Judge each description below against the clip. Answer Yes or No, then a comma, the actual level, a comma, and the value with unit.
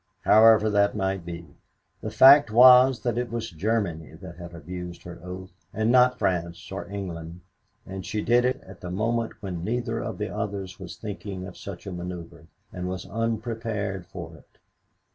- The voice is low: Yes, low, 100 Hz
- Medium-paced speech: Yes, average, 175 wpm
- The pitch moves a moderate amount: Yes, average, 4.1 semitones